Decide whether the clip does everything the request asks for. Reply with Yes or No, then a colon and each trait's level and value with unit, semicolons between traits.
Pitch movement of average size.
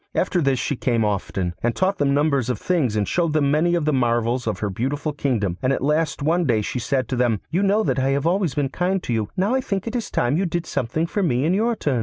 No: wide, 6.2 semitones